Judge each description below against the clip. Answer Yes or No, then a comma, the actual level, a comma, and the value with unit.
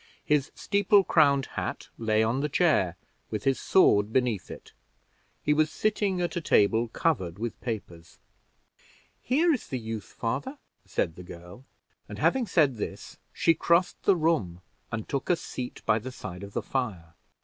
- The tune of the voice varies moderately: No, wide, 7.6 semitones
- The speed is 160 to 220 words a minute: Yes, average, 165 wpm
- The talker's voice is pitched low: Yes, low, 130 Hz